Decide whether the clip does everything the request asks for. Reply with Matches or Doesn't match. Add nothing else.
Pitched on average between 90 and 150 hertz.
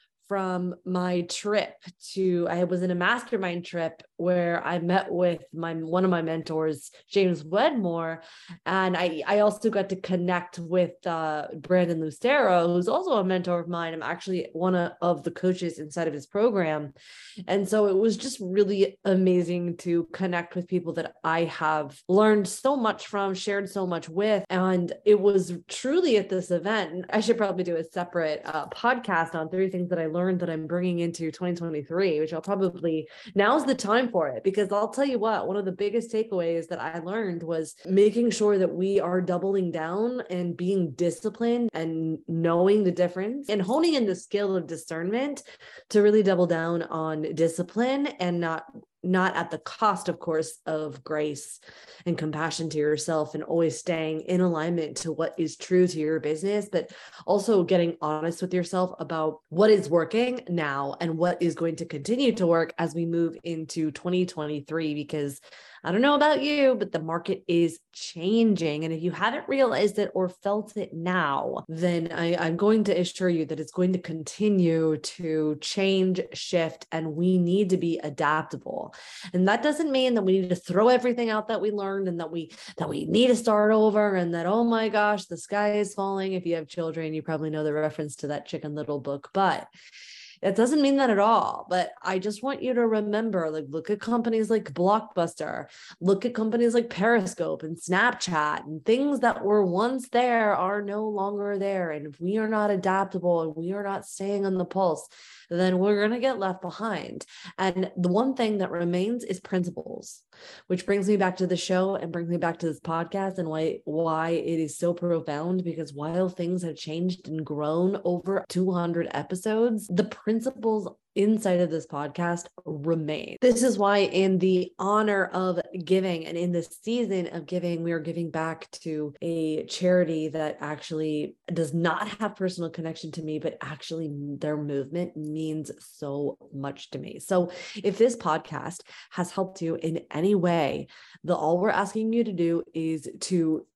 Doesn't match